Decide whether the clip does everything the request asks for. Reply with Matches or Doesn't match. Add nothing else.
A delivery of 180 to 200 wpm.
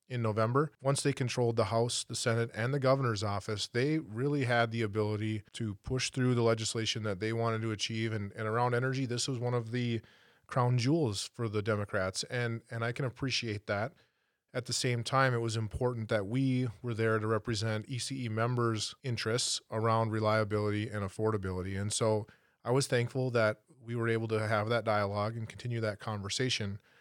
Matches